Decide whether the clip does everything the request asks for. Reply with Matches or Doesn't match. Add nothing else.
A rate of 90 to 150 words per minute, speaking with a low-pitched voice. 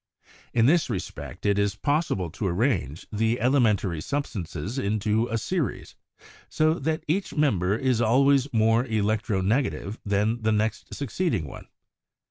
Matches